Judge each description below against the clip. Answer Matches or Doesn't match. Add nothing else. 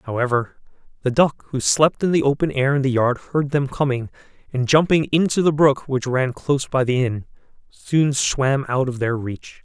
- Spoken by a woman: Doesn't match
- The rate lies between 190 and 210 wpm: Matches